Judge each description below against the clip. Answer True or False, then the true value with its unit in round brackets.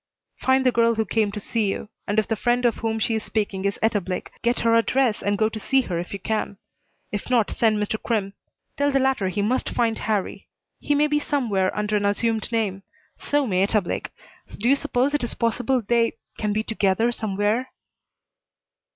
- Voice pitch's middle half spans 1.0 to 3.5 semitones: True (2.9 semitones)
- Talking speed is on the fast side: True (210 wpm)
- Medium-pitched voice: False (220 Hz)